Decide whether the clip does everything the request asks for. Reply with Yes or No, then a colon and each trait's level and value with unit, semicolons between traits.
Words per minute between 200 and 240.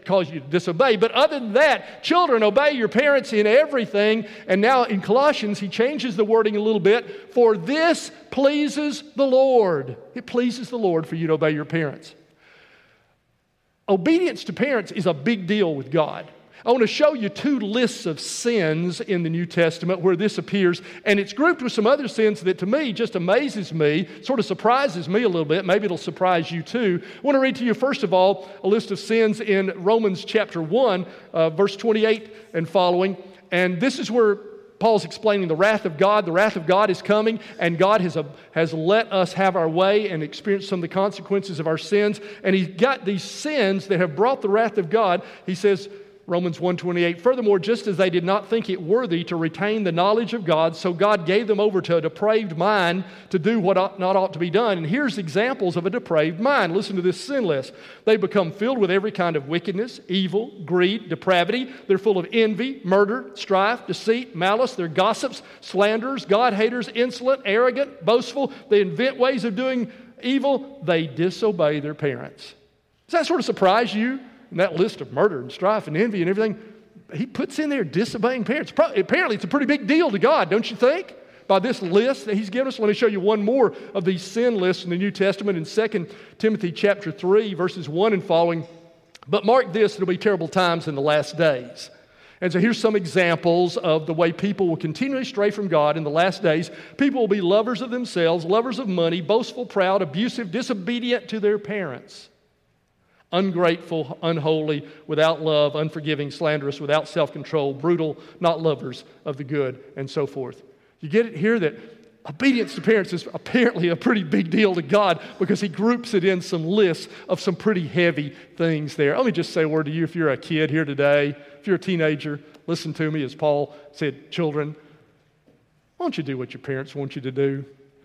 Yes: fast, 205 wpm